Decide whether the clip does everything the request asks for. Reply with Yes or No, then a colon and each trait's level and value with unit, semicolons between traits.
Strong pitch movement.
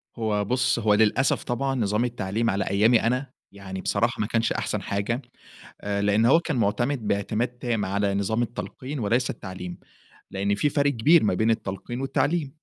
No: average, 3.6 semitones